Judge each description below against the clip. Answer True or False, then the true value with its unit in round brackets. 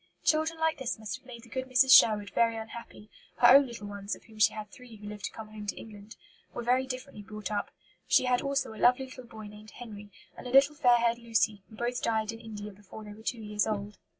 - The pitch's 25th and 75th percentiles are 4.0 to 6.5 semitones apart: False (3.1 semitones)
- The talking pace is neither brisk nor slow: False (250 wpm)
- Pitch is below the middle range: False (225 Hz)